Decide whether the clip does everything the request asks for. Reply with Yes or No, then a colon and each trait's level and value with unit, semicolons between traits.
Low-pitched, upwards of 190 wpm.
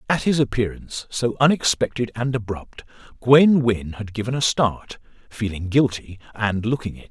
No: low, 115 Hz; average, 145 wpm